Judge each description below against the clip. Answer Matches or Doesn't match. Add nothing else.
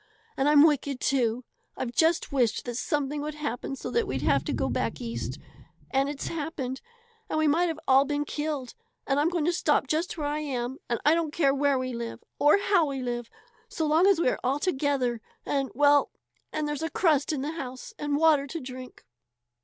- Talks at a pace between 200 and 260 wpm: Matches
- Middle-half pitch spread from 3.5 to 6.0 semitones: Doesn't match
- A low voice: Doesn't match